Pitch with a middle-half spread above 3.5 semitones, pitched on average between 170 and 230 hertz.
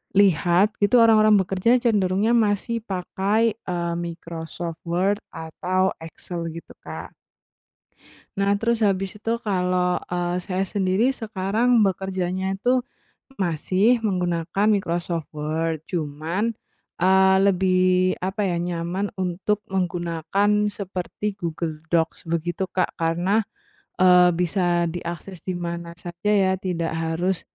No: average, 2.8 semitones; medium, 185 Hz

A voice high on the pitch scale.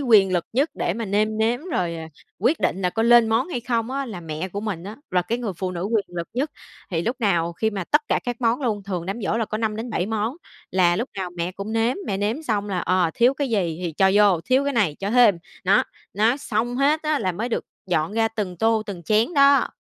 Yes: high, 215 Hz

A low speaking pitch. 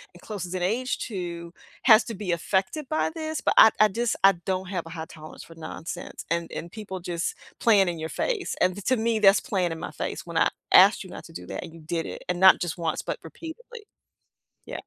No: high, 190 Hz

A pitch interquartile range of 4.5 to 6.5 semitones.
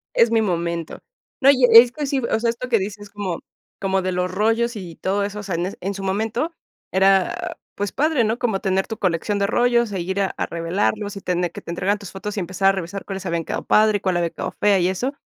No: average, 3.2 semitones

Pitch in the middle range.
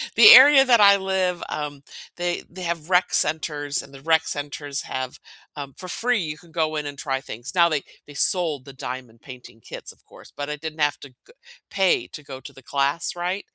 Yes: medium, 155 Hz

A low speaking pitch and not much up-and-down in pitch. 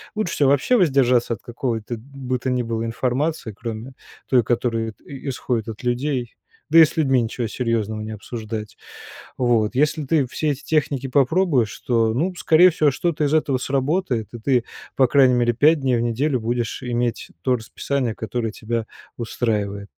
No: low, 125 Hz; average, 3.5 semitones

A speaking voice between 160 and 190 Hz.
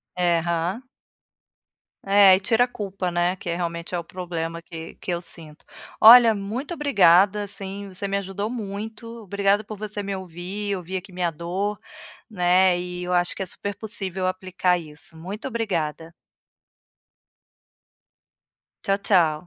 Yes: medium, 185 Hz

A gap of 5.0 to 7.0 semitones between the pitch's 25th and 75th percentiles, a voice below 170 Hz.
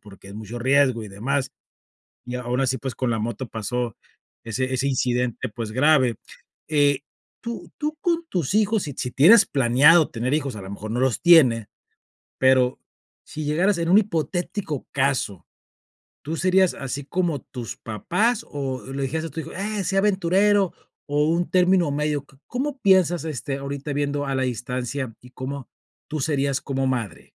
Yes: wide, 5.4 semitones; medium, 140 Hz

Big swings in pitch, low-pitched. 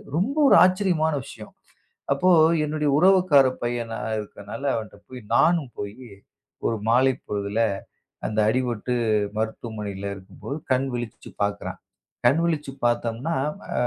Yes: wide, 5.9 semitones; low, 125 Hz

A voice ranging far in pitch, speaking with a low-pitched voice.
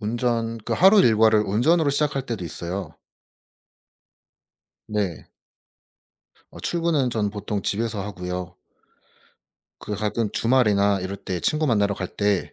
No: average, 3.4 semitones; low, 105 Hz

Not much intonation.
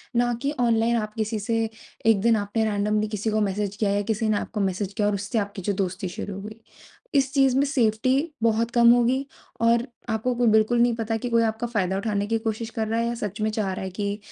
Yes: narrow, 2.3 semitones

